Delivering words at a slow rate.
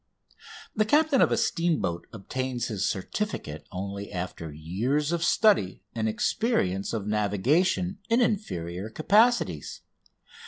Yes: slow, 115 wpm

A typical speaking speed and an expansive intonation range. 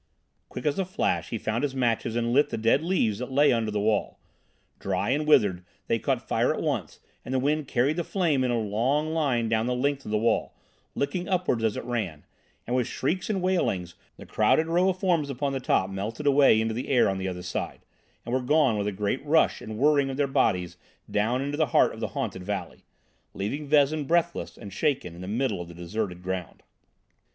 No: fast, 220 wpm; wide, 5.8 semitones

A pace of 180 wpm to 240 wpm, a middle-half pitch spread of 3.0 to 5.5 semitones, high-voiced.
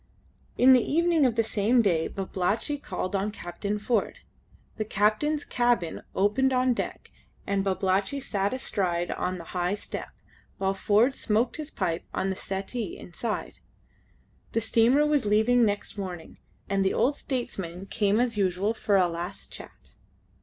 No: average, 155 wpm; average, 4.2 semitones; high, 210 Hz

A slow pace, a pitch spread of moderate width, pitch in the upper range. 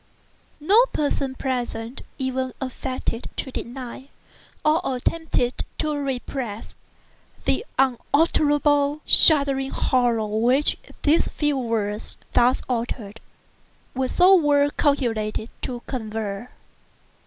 Yes: slow, 95 wpm; average, 3.4 semitones; very high, 260 Hz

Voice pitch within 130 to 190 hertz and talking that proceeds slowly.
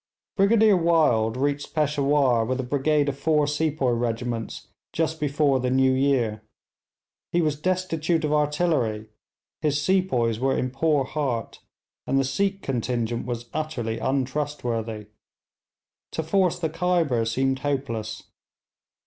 Yes: medium, 140 Hz; slow, 125 wpm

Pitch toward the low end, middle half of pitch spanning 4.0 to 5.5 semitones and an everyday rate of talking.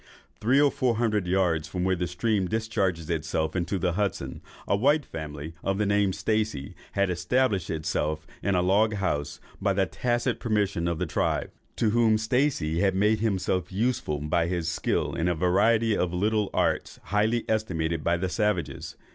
Yes: very low, 95 Hz; average, 4.3 semitones; average, 175 wpm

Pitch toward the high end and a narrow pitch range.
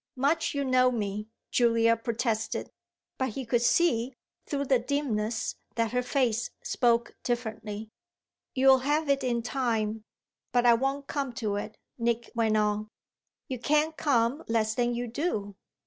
No: high, 240 Hz; average, 3.1 semitones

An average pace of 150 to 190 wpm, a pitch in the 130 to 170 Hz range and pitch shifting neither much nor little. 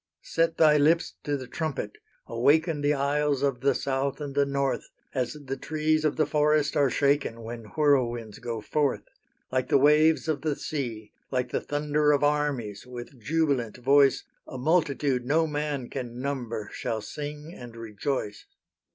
Yes: average, 160 wpm; medium, 140 Hz; average, 3.1 semitones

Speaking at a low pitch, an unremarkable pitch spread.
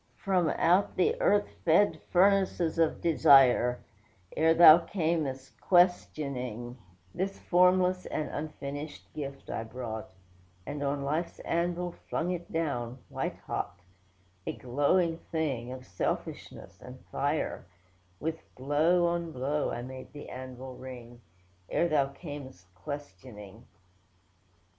No: medium, 145 Hz; average, 5.0 semitones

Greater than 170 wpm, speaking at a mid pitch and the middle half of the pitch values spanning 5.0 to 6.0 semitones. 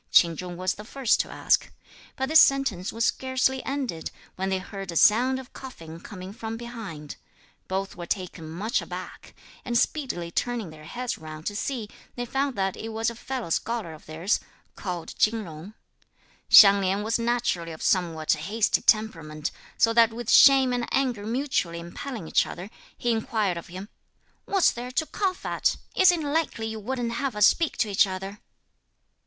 No: average, 180 wpm; high, 220 Hz; wide, 5.5 semitones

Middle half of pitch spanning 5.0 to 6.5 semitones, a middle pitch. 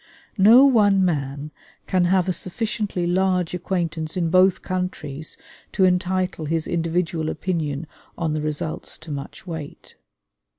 No: average, 2.9 semitones; medium, 175 Hz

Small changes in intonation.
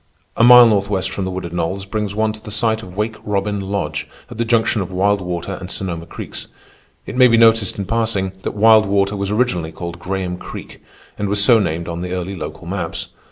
No: average, 3.0 semitones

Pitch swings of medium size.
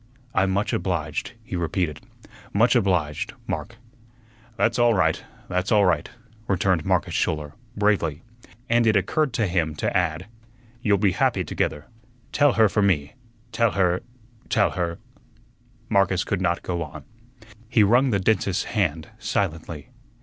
Yes: average, 4.7 semitones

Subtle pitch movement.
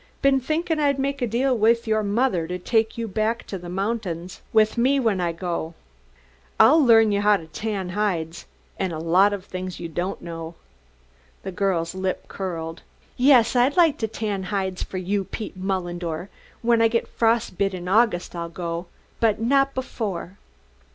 No: average, 4.5 semitones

